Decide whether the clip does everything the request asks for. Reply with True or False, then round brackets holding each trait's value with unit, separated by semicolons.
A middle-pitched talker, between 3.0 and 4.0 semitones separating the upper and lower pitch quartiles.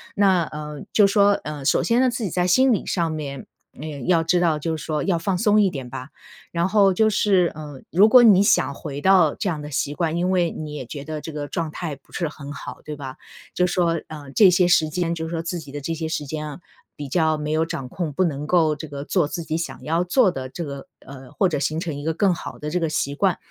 True (160 Hz; 3.3 semitones)